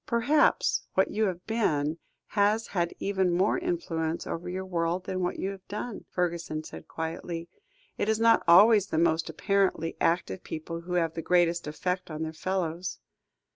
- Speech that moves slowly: No, average, 170 wpm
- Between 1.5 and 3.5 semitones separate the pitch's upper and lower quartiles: Yes, average, 3.1 semitones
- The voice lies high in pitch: No, medium, 180 Hz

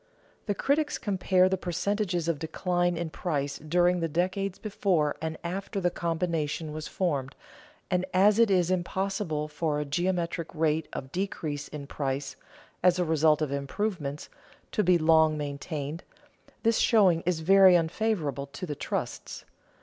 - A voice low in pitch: No, medium, 170 Hz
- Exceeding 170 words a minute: No, average, 150 wpm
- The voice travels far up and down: No, average, 3.6 semitones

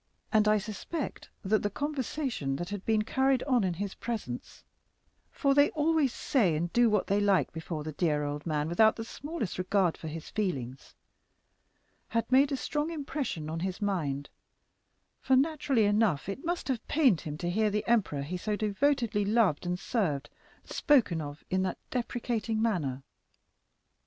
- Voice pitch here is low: No, high, 210 Hz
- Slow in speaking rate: No, average, 165 wpm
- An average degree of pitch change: No, wide, 7.0 semitones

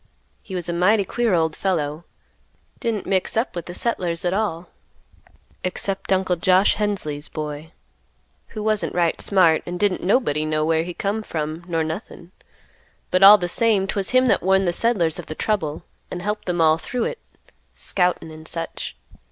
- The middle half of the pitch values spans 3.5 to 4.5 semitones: Yes, average, 3.9 semitones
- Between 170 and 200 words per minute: Yes, average, 175 wpm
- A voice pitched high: No, medium, 180 Hz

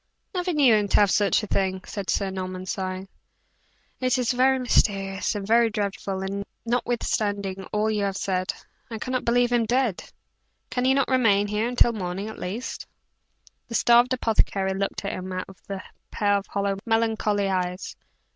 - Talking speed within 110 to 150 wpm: No, average, 175 wpm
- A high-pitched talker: Yes, high, 205 Hz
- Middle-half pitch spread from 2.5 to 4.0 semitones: Yes, average, 3.6 semitones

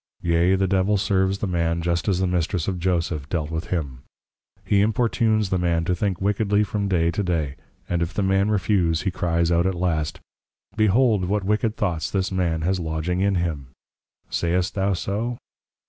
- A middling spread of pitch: Yes, average, 3.0 semitones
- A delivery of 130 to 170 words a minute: No, average, 190 wpm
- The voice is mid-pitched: No, very low, 90 Hz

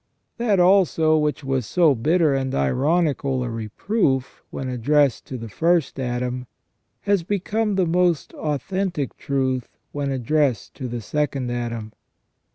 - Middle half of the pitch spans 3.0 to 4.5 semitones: No, average, 5.3 semitones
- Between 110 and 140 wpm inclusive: Yes, slow, 135 wpm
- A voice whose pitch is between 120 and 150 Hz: Yes, medium, 140 Hz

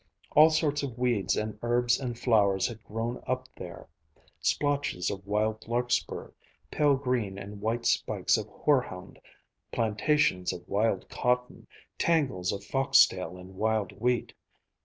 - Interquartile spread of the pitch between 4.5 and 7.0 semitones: No, average, 4.0 semitones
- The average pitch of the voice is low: Yes, low, 115 Hz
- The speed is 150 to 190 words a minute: No, slow, 135 wpm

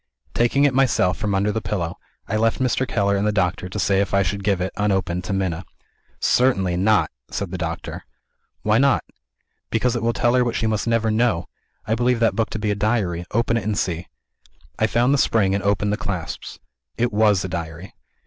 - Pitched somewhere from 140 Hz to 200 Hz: No, low, 105 Hz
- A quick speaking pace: Yes, fast, 215 wpm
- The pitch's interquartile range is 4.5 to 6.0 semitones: No, average, 3.4 semitones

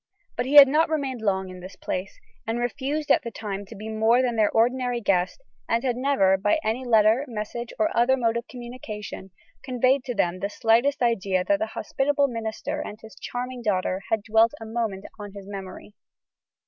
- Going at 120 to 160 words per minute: No, average, 195 wpm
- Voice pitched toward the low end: No, high, 230 Hz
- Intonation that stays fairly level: No, average, 3.7 semitones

